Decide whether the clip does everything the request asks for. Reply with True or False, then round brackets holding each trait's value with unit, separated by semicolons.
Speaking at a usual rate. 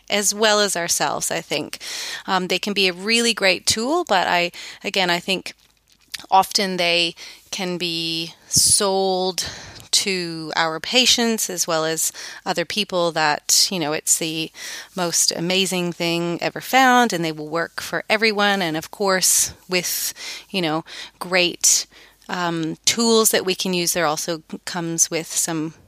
True (155 wpm)